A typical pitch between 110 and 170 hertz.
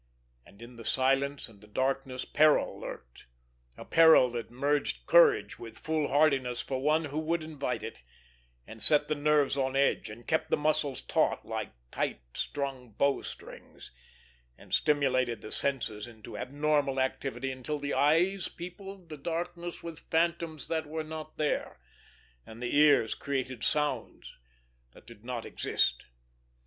Yes: medium, 140 Hz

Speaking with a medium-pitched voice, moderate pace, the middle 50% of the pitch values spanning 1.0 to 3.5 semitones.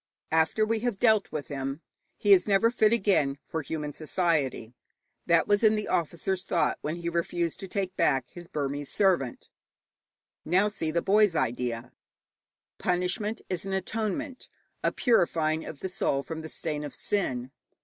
No: medium, 175 Hz; average, 160 wpm; average, 5.3 semitones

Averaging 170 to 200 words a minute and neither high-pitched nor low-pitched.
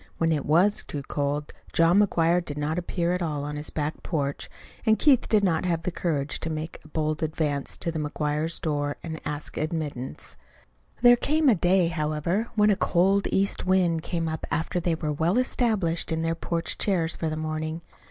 Yes: average, 195 wpm; medium, 165 Hz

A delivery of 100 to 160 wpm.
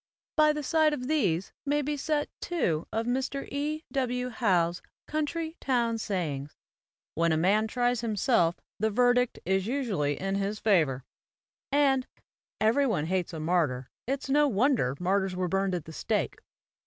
Yes: average, 155 wpm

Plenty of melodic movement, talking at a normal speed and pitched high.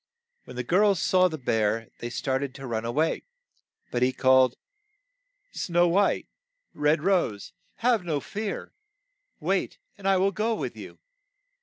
No: wide, 7.3 semitones; average, 155 wpm; medium, 155 Hz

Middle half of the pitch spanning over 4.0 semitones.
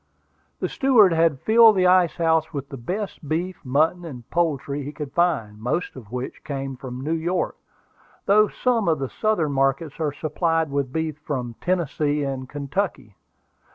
Yes: average, 4.4 semitones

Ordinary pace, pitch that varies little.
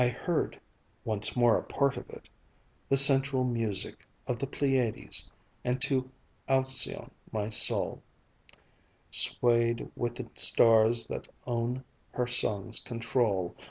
No: slow, 125 wpm; narrow, 2.3 semitones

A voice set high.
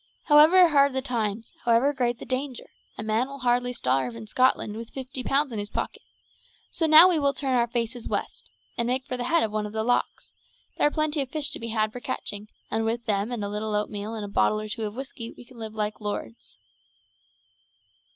Yes: high, 235 Hz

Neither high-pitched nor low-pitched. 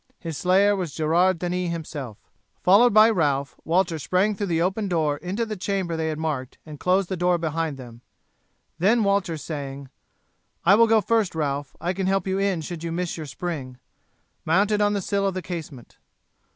Yes: medium, 175 Hz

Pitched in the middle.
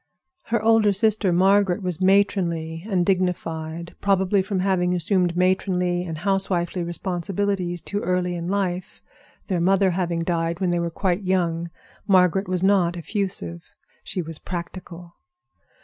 Yes: medium, 180 Hz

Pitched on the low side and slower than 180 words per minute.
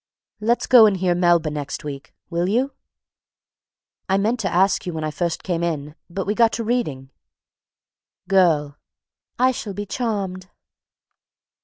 No: medium, 185 Hz; average, 155 wpm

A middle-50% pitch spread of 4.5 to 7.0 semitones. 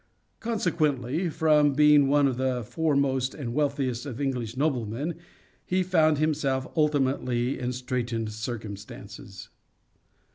No: average, 3.6 semitones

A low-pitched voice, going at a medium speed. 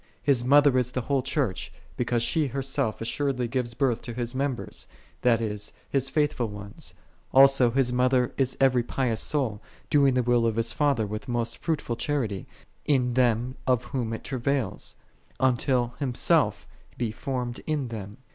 Yes: low, 125 Hz; average, 160 wpm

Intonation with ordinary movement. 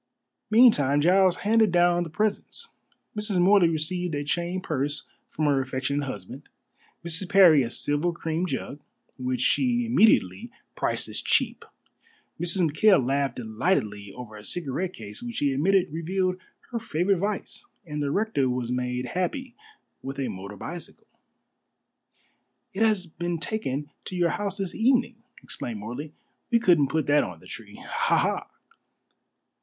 No: wide, 6.1 semitones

